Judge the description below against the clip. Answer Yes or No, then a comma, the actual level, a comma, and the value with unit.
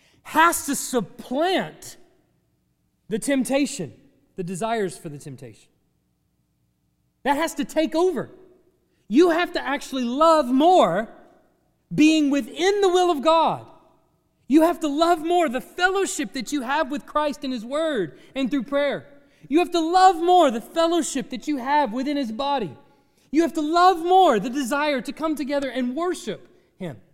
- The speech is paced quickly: No, average, 155 wpm